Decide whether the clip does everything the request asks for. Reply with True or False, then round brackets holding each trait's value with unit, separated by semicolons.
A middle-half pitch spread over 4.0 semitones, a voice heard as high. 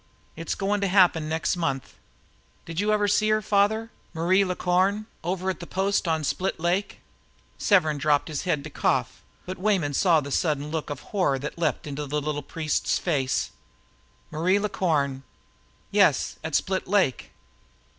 False (4.5 semitones; 170 Hz)